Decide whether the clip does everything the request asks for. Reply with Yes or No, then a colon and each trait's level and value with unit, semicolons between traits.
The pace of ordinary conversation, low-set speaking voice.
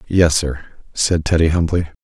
Yes: average, 150 wpm; very low, 80 Hz